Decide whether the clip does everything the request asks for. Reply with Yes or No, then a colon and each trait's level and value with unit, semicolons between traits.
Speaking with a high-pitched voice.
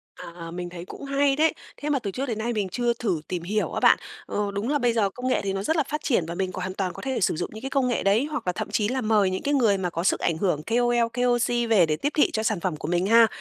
Yes: high, 220 Hz